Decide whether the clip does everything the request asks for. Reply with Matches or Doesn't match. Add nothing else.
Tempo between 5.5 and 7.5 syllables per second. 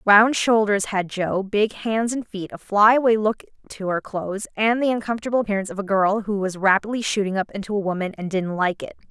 Matches